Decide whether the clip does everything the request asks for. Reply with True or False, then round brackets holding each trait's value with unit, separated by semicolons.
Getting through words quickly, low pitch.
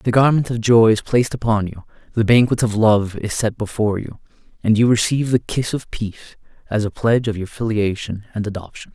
True (210 wpm; 110 Hz)